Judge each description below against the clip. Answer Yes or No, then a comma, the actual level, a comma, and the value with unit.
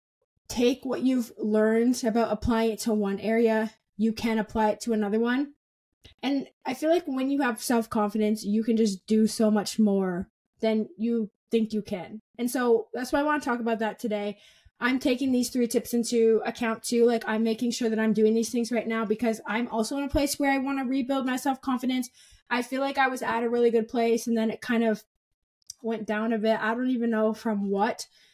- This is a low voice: No, high, 230 Hz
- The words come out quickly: Yes, fast, 220 wpm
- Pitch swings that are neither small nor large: No, narrow, 2.3 semitones